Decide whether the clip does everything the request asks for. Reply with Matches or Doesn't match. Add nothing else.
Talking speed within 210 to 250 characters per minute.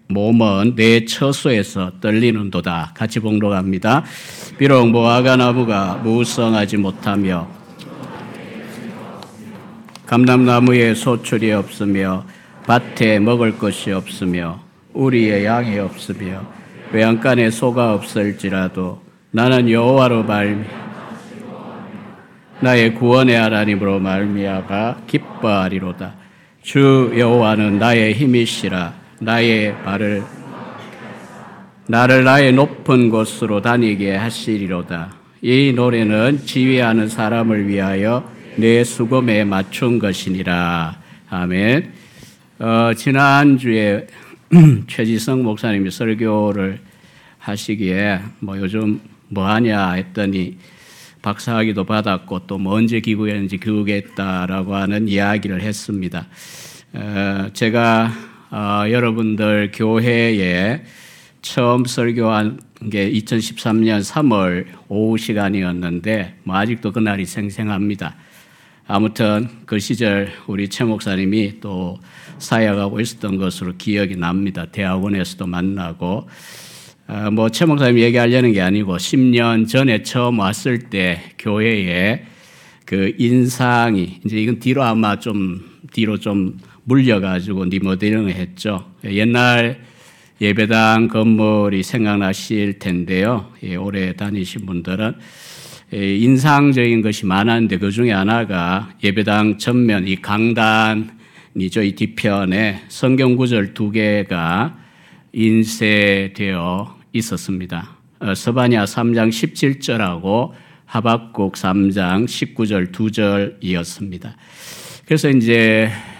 Matches